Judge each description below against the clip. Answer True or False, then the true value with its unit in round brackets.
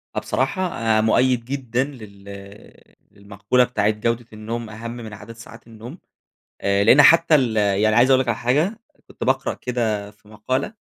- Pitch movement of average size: True (3.4 semitones)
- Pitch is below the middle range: True (115 Hz)